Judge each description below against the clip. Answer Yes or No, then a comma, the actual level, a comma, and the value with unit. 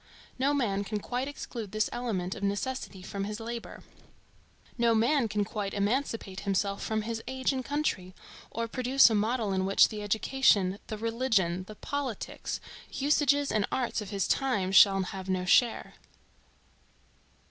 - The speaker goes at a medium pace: Yes, average, 155 wpm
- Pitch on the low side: No, high, 220 Hz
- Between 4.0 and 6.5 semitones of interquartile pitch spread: Yes, average, 4.3 semitones